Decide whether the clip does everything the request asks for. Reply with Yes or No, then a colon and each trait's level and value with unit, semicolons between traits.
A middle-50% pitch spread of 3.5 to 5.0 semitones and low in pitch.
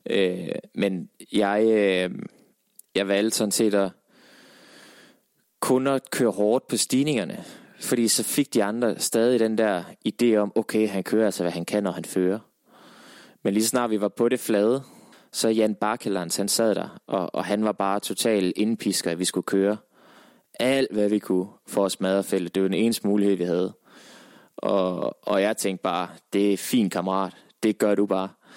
No: average, 2.8 semitones; low, 105 Hz